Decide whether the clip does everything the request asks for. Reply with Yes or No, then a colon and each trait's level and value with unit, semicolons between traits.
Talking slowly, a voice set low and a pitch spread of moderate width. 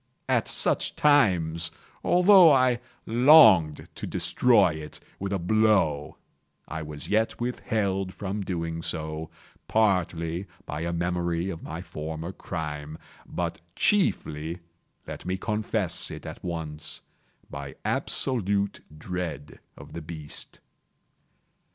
Yes: slow, 110 wpm; very low, 90 Hz; average, 4.8 semitones